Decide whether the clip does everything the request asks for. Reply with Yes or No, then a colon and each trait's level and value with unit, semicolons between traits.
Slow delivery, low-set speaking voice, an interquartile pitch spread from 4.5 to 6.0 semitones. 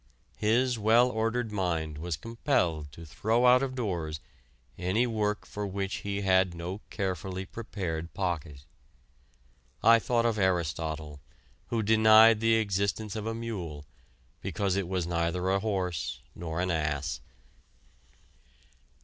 Yes: slow, 130 wpm; very low, 95 Hz; average, 4.8 semitones